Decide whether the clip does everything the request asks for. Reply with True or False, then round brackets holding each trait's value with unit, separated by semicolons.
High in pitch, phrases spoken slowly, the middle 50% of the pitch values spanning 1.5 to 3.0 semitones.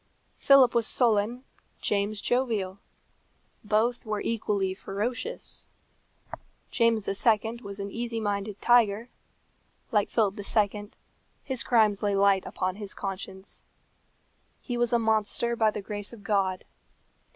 True (210 Hz; 120 wpm; 2.6 semitones)